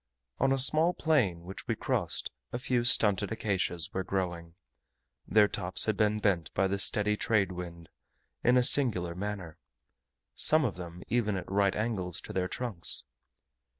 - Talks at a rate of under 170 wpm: Yes, average, 160 wpm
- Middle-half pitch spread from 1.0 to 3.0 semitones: No, average, 4.5 semitones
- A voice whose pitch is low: Yes, low, 100 Hz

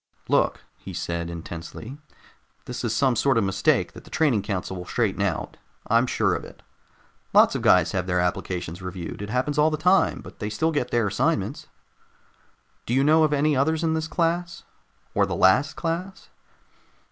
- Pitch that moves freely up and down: Yes, wide, 8.6 semitones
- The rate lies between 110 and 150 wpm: No, average, 180 wpm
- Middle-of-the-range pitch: No, low, 120 Hz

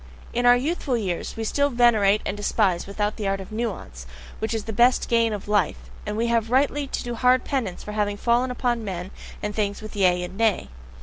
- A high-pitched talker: Yes, high, 220 Hz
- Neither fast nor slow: No, fast, 220 wpm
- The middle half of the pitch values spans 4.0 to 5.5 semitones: No, average, 3.1 semitones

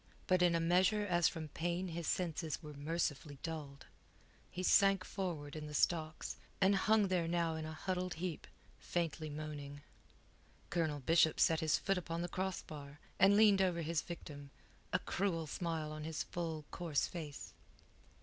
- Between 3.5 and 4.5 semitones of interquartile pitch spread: No, average, 2.8 semitones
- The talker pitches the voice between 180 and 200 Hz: No, medium, 165 Hz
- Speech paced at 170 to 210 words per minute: No, average, 160 wpm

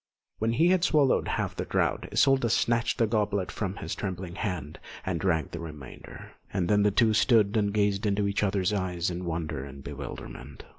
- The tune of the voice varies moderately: Yes, average, 4.0 semitones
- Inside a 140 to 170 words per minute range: No, average, 190 wpm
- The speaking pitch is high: No, low, 100 Hz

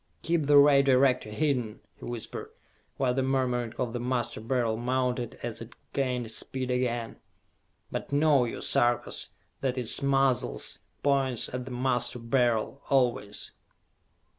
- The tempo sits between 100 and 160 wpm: Yes, average, 140 wpm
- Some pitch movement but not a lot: No, narrow, 2.1 semitones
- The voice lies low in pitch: Yes, low, 125 Hz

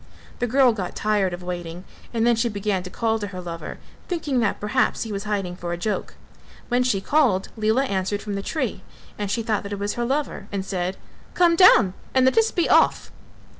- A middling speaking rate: No, fast, 215 wpm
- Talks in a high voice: Yes, high, 210 Hz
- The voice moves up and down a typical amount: Yes, average, 4.3 semitones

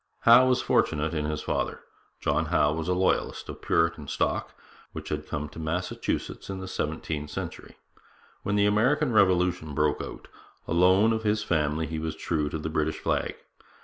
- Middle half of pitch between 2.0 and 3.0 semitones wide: No, average, 4.5 semitones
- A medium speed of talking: Yes, average, 175 wpm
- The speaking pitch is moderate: No, very low, 80 Hz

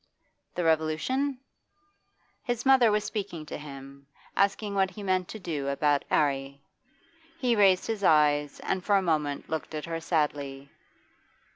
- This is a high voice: No, medium, 165 Hz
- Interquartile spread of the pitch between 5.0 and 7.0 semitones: Yes, wide, 5.6 semitones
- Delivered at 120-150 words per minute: Yes, average, 145 wpm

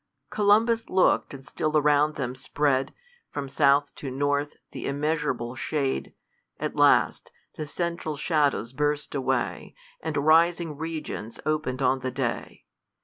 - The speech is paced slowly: Yes, slow, 130 wpm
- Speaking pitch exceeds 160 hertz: No, medium, 145 Hz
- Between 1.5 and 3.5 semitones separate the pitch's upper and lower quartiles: Yes, narrow, 2.6 semitones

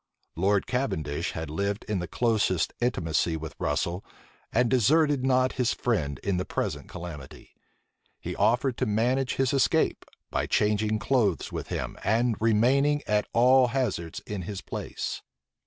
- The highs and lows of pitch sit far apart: Yes, wide, 6.1 semitones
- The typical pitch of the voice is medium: No, low, 110 Hz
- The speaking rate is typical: Yes, average, 145 wpm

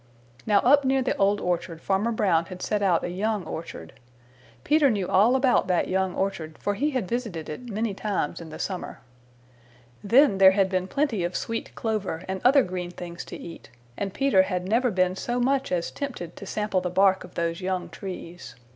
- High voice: Yes, high, 195 Hz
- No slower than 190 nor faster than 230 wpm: Yes, average, 200 wpm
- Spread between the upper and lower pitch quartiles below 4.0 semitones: No, average, 4.3 semitones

